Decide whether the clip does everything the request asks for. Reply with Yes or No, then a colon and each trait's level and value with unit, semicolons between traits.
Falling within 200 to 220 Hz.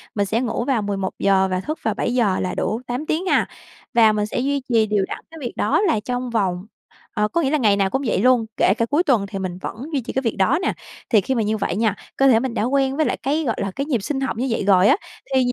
No: high, 230 Hz